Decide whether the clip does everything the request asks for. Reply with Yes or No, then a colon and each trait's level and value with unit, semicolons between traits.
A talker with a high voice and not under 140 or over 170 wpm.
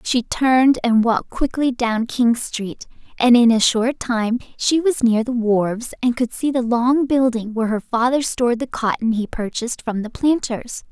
No: high, 240 Hz; average, 190 wpm